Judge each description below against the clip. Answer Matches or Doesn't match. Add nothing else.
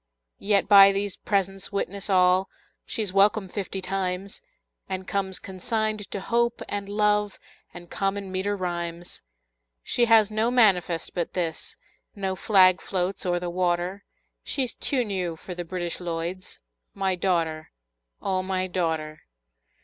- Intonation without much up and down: Matches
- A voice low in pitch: Doesn't match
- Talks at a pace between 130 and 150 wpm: Matches